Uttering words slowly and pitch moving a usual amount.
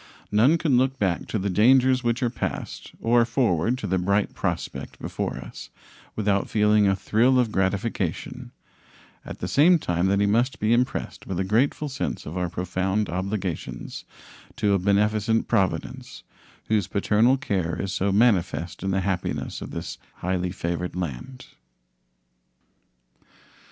No: average, 150 wpm; average, 4.1 semitones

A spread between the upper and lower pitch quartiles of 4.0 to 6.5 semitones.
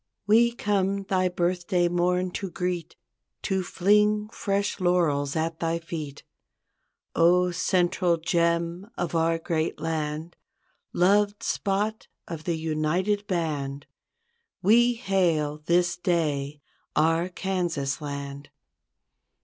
No: average, 3.1 semitones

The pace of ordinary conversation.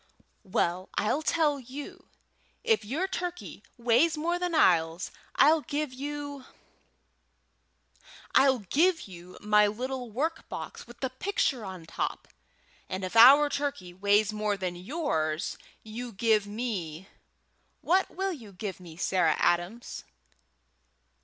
No: slow, 125 wpm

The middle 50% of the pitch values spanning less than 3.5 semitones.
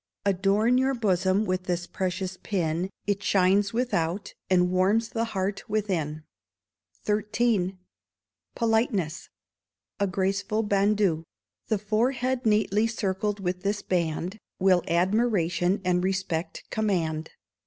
Yes: average, 2.9 semitones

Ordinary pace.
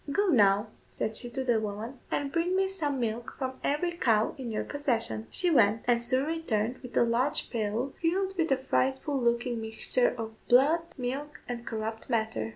Yes: average, 185 wpm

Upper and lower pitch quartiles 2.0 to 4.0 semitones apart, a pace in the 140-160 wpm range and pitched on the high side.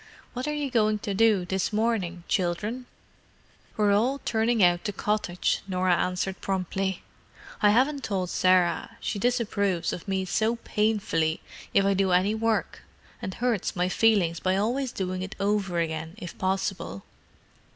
Yes: average, 3.4 semitones; average, 150 wpm; high, 195 Hz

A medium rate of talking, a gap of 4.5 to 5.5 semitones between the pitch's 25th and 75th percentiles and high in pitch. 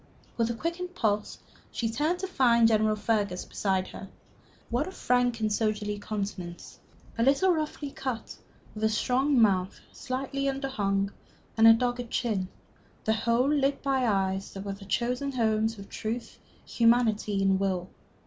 No: average, 155 wpm; average, 4.1 semitones; high, 225 Hz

